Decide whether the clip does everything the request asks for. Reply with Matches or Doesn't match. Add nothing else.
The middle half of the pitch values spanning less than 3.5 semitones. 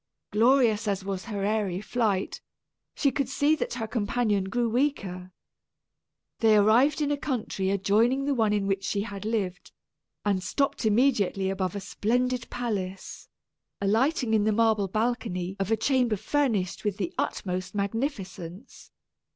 Doesn't match